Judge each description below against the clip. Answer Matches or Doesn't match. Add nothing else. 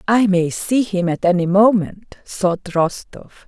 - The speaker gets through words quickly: Doesn't match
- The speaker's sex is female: Matches